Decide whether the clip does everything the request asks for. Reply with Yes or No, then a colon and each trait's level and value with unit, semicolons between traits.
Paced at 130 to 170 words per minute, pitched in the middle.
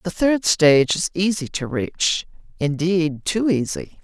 Yes: slow, 135 wpm; medium, 170 Hz